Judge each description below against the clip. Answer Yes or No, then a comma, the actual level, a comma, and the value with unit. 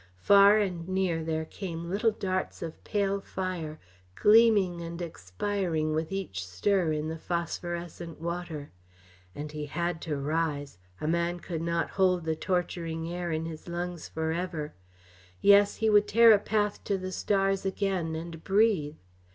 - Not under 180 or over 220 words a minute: No, average, 155 wpm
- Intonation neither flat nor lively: Yes, average, 3.3 semitones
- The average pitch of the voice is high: No, medium, 170 Hz